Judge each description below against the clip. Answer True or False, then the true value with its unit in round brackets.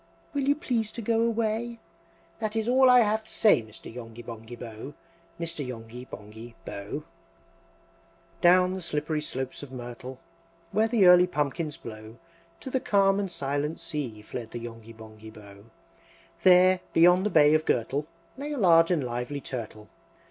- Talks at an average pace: True (165 wpm)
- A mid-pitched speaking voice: True (150 Hz)